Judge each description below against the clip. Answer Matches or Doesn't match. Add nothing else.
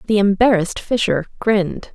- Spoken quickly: Doesn't match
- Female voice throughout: Matches